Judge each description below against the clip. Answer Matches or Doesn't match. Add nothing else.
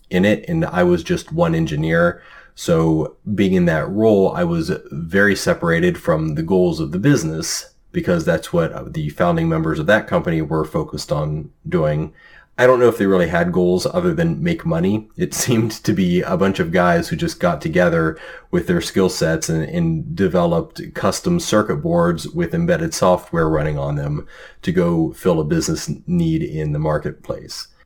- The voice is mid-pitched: Matches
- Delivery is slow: Doesn't match